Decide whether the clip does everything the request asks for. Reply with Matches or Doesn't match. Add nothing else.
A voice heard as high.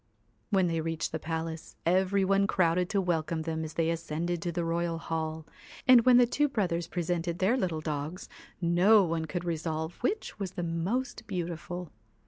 Doesn't match